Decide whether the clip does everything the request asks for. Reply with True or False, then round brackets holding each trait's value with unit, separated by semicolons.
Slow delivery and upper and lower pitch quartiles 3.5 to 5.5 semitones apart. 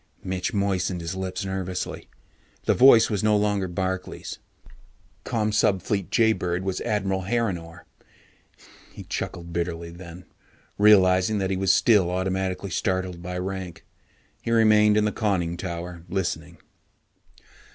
False (120 wpm; 2.5 semitones)